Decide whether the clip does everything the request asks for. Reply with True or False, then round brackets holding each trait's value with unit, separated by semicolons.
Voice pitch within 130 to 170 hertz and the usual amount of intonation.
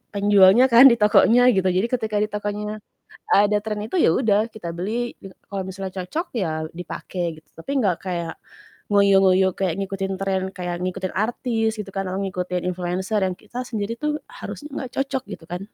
False (200 Hz; 3.2 semitones)